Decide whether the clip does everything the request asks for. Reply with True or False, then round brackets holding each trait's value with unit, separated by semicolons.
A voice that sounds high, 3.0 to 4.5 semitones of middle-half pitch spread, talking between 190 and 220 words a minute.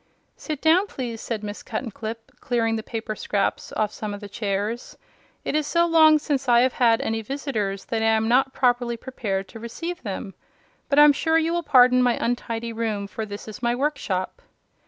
True (235 Hz; 4.2 semitones; 195 wpm)